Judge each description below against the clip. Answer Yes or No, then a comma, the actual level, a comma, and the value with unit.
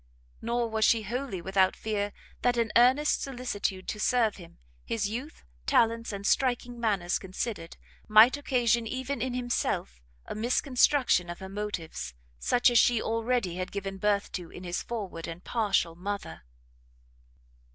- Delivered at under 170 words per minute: Yes, average, 150 wpm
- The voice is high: Yes, high, 220 Hz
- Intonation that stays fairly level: No, average, 4.2 semitones